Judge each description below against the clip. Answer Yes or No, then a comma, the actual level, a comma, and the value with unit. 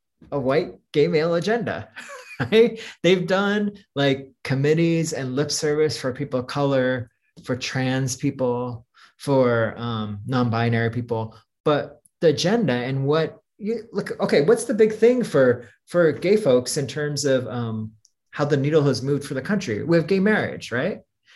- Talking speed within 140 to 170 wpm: Yes, average, 160 wpm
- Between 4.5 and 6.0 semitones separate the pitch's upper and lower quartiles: Yes, average, 5.2 semitones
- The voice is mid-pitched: Yes, medium, 145 Hz